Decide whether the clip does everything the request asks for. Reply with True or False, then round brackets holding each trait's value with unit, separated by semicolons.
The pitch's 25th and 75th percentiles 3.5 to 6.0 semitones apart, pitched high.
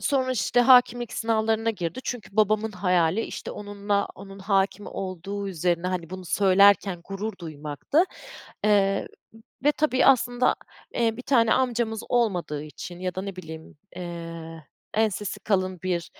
True (3.9 semitones; 200 Hz)